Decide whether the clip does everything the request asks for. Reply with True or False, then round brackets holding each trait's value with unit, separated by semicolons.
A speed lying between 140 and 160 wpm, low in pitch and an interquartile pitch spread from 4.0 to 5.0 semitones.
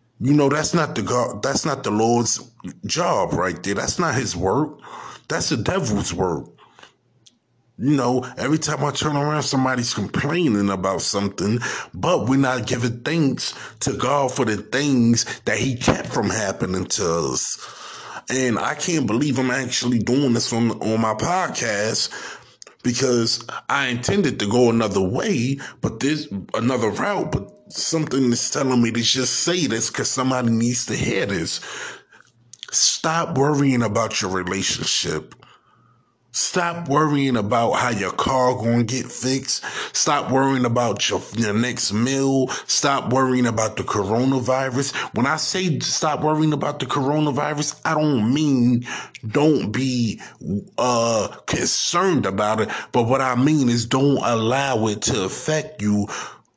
False (150 wpm; 125 Hz; 3.4 semitones)